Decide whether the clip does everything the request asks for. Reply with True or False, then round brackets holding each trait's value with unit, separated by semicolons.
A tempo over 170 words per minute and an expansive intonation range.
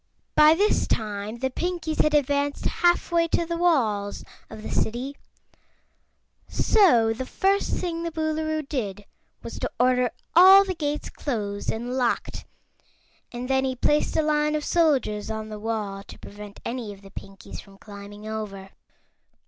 False (155 wpm; 6.7 semitones)